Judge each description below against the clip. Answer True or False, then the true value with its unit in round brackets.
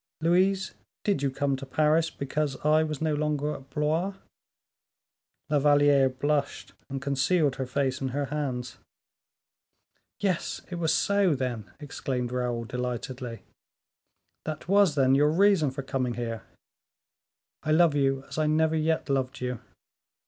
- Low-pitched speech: False (145 Hz)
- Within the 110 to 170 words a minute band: True (140 wpm)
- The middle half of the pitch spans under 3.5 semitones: True (3.0 semitones)